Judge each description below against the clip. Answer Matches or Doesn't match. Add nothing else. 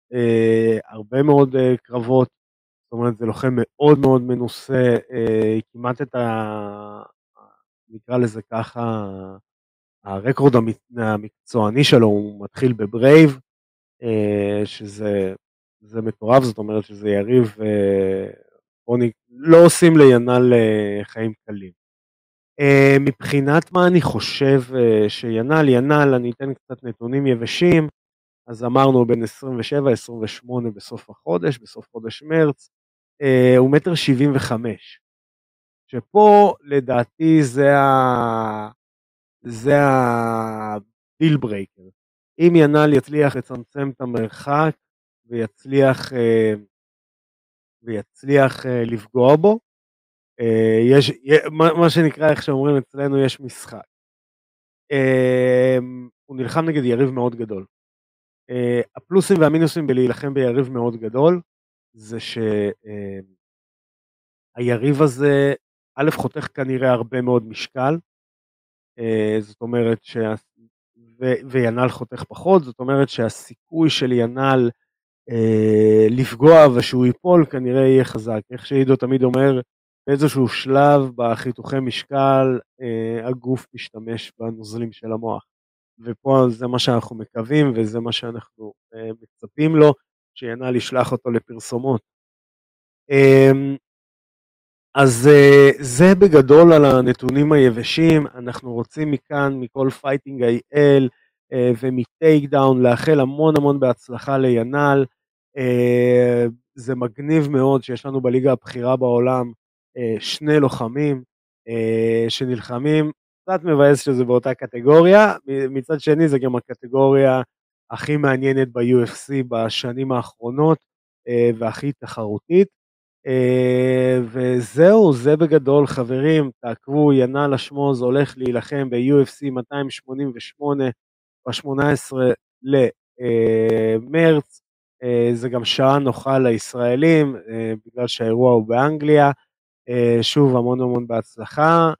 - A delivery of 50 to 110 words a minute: Matches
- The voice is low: Matches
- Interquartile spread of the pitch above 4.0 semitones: Doesn't match